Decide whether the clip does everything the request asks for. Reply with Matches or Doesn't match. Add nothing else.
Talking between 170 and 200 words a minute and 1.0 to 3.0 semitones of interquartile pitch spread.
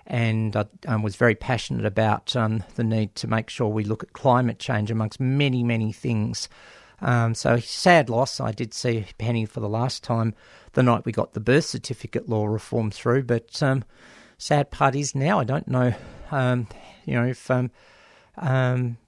Matches